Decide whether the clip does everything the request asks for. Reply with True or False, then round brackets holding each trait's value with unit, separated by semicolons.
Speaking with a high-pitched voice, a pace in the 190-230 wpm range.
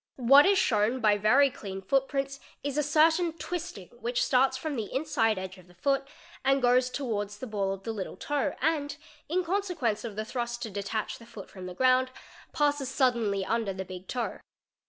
True (245 Hz; 200 wpm)